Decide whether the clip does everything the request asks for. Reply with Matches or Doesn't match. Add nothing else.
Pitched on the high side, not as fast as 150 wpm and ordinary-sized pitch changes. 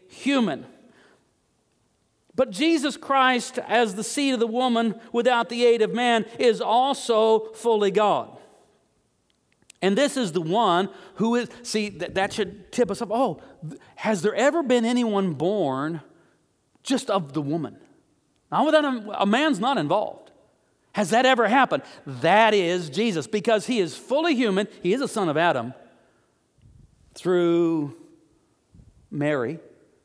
Matches